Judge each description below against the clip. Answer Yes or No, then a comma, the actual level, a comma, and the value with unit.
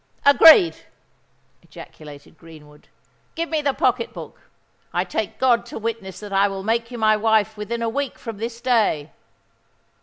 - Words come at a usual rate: Yes, average, 150 wpm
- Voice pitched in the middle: No, high, 225 Hz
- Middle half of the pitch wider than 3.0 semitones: Yes, average, 3.8 semitones